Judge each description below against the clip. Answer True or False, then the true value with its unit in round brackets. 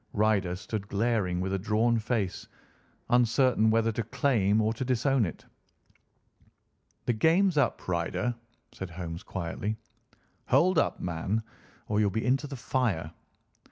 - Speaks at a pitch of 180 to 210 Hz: False (110 Hz)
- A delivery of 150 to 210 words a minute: False (135 wpm)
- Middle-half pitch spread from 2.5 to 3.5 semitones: False (4.2 semitones)